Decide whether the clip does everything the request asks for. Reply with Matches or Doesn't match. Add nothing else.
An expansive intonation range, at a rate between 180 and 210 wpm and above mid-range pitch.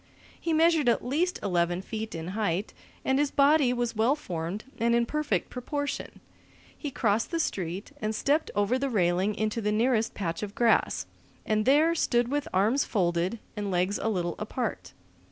Doesn't match